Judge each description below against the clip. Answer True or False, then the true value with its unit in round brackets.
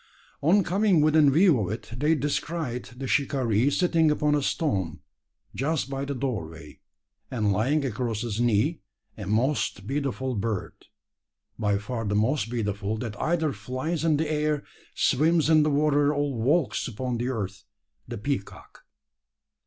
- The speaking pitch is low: True (130 Hz)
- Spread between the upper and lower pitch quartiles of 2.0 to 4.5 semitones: False (5.6 semitones)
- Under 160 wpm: True (150 wpm)